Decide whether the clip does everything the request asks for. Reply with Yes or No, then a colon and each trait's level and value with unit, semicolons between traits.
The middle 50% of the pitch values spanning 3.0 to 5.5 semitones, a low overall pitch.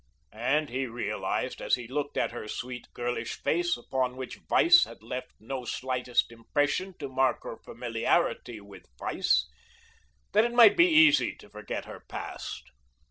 Yes: average, 4.4 semitones; low, 130 Hz